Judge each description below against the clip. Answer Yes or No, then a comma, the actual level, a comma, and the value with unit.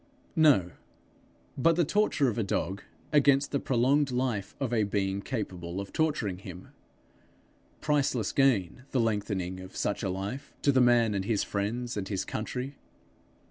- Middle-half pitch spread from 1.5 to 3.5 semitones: No, wide, 5.5 semitones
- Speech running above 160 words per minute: No, average, 155 wpm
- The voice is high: No, low, 115 Hz